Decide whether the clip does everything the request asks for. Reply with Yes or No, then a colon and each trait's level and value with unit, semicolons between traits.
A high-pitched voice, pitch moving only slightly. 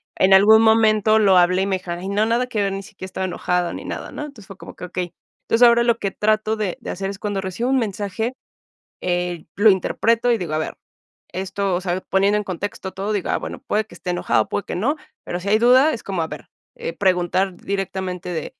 No: high, 195 Hz; average, 3.0 semitones